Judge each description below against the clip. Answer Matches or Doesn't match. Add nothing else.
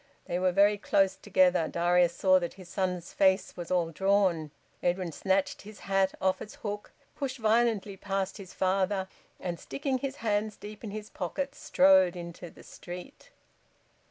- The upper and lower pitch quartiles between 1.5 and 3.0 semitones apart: Matches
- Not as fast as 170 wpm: Matches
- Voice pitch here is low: Doesn't match